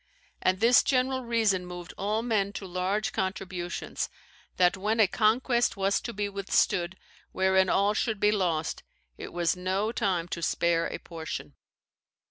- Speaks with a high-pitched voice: Yes, high, 195 Hz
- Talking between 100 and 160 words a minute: Yes, average, 150 wpm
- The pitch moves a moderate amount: Yes, average, 3.0 semitones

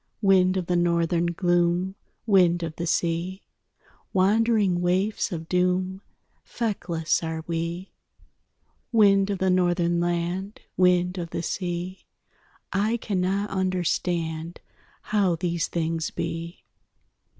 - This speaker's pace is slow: Yes, slow, 110 wpm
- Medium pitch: Yes, medium, 180 Hz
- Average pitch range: No, narrow, 1.9 semitones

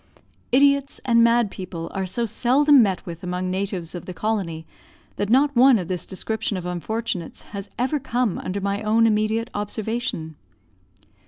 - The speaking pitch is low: No, high, 215 Hz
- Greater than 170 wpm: No, average, 160 wpm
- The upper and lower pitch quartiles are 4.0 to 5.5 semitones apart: Yes, average, 4.4 semitones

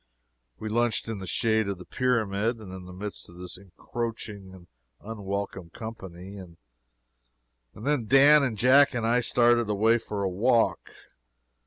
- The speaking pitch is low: Yes, low, 110 Hz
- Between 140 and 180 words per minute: Yes, average, 155 wpm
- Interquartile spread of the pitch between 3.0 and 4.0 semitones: Yes, average, 3.7 semitones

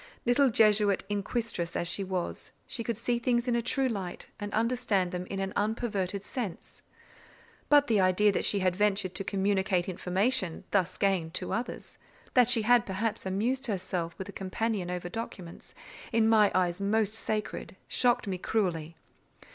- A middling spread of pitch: Yes, average, 3.6 semitones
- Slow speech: No, average, 165 wpm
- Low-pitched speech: No, high, 205 Hz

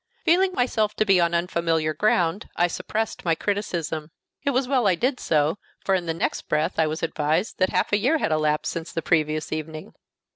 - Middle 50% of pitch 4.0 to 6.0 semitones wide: Yes, average, 5.1 semitones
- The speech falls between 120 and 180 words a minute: No, fast, 205 wpm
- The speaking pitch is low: No, medium, 170 Hz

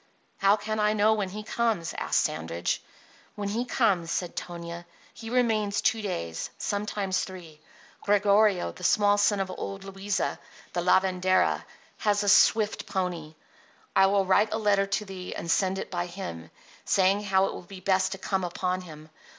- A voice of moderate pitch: No, high, 195 Hz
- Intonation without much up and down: Yes, narrow, 2.3 semitones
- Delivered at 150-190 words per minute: Yes, average, 170 wpm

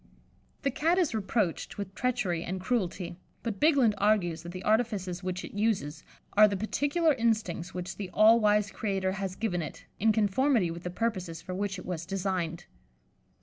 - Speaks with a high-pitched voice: Yes, high, 200 Hz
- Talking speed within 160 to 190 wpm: Yes, average, 175 wpm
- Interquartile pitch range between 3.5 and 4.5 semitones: Yes, average, 3.8 semitones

